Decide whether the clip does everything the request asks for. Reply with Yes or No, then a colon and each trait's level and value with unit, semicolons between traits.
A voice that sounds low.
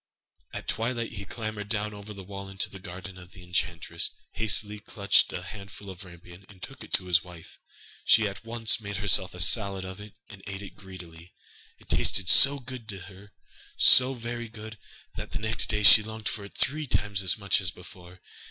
Yes: low, 100 Hz